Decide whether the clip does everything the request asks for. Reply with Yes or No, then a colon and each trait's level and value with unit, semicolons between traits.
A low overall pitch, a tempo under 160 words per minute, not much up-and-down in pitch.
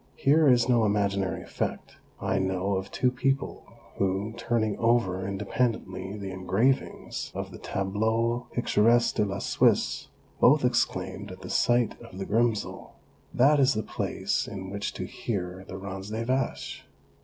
No: low, 105 Hz; average, 150 wpm; average, 3.8 semitones